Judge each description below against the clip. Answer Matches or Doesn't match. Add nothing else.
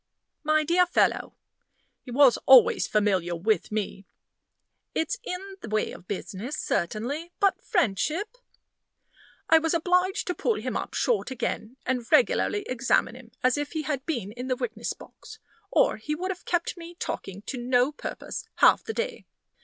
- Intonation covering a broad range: Matches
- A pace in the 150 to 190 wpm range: Matches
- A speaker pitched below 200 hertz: Doesn't match